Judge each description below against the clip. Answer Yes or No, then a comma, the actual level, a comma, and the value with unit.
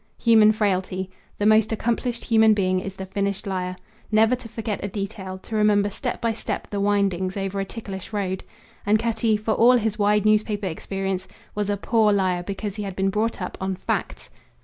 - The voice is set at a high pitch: Yes, high, 205 Hz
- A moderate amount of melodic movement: No, narrow, 2.2 semitones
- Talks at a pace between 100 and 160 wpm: No, average, 195 wpm